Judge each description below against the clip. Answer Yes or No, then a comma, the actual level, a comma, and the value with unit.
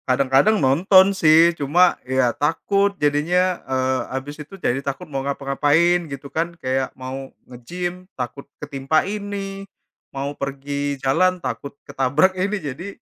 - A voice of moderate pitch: Yes, medium, 145 Hz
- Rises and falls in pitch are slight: No, average, 5.0 semitones